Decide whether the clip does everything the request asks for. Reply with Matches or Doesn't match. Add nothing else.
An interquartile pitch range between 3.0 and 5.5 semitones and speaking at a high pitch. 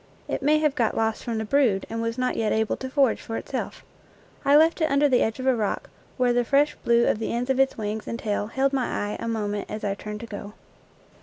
Matches